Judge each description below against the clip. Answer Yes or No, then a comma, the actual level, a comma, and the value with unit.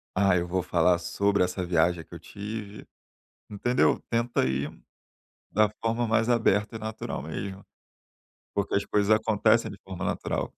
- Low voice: Yes, low, 100 Hz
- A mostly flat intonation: No, average, 3.4 semitones